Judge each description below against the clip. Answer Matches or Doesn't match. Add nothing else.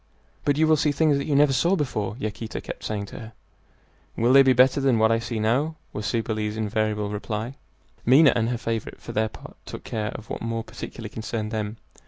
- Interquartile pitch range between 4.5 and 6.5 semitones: Doesn't match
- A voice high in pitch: Doesn't match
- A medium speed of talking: Doesn't match